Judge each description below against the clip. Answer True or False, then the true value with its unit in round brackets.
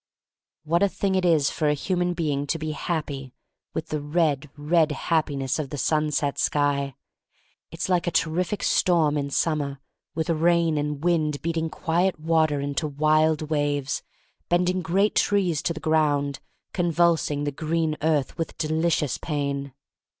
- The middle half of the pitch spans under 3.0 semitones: True (2.5 semitones)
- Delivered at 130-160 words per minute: True (155 wpm)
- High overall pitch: False (155 Hz)